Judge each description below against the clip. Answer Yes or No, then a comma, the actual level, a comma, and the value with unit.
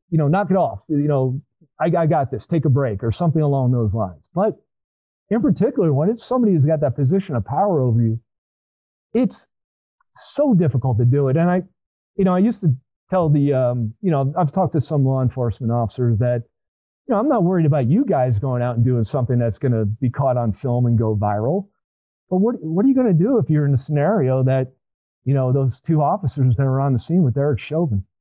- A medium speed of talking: No, fast, 230 wpm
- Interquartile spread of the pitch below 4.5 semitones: No, wide, 5.4 semitones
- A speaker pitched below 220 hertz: Yes, low, 135 Hz